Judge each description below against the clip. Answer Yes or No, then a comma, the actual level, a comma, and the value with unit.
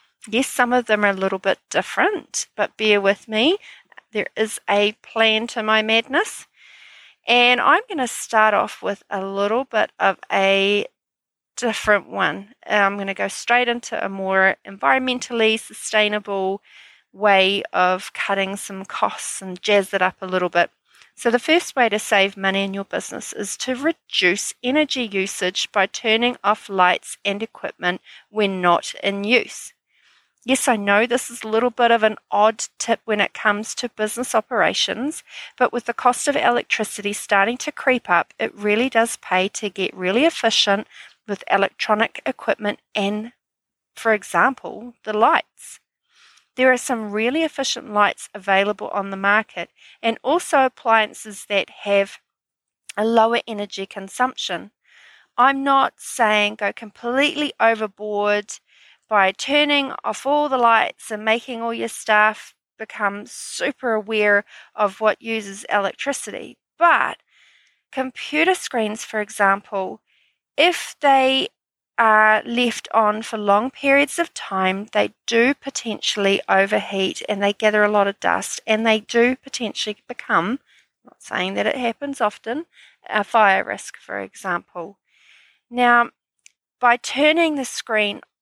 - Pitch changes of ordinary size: Yes, average, 3.5 semitones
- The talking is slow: No, average, 145 wpm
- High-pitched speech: Yes, high, 220 Hz